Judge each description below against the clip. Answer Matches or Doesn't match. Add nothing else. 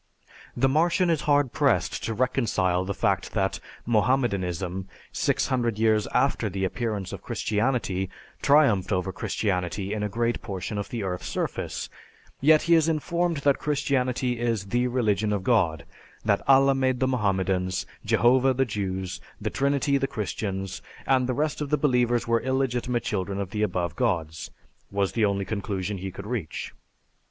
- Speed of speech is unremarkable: Matches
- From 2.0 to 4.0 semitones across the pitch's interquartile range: Doesn't match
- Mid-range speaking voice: Doesn't match